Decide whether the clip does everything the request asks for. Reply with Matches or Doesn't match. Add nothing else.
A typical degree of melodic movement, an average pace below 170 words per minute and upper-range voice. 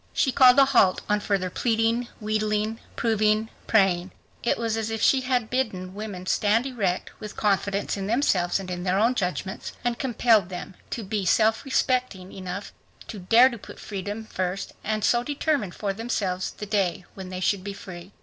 Doesn't match